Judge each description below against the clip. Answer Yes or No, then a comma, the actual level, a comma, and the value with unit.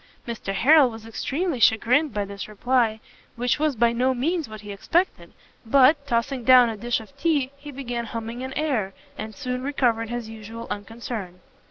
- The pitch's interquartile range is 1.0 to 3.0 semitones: No, average, 3.6 semitones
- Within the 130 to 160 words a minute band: No, average, 175 wpm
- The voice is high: Yes, high, 240 Hz